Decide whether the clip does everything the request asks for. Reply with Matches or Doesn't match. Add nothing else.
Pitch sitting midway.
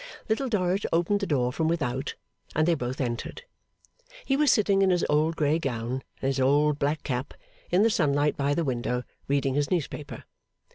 Matches